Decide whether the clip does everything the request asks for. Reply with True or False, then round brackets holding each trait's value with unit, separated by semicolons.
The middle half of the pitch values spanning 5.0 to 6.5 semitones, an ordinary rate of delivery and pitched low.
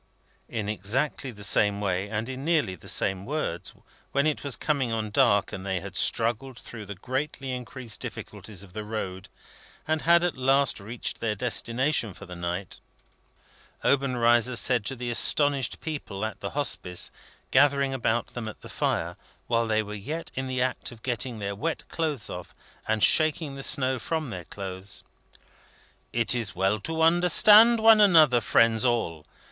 True (5.3 semitones; 170 wpm; 120 Hz)